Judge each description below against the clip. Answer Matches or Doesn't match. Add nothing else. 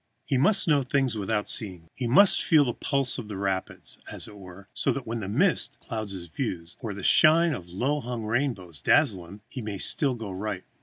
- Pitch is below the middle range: Matches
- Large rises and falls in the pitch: Matches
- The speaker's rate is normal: Doesn't match